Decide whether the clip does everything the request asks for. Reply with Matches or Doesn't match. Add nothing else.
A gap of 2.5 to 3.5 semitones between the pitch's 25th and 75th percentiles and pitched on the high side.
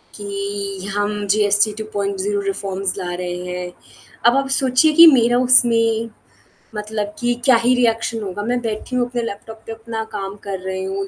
Matches